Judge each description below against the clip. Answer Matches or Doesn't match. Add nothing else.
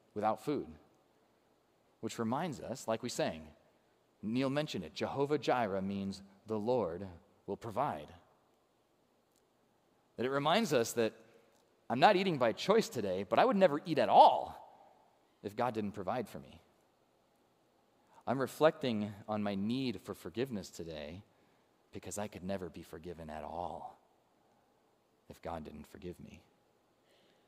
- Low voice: Matches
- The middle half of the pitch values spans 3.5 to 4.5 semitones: Matches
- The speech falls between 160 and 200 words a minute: Doesn't match